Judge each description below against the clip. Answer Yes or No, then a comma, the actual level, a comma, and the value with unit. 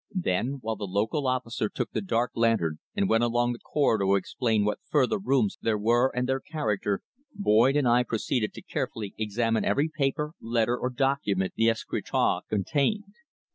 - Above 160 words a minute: Yes, average, 175 wpm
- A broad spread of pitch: No, average, 3.9 semitones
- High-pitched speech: No, low, 120 Hz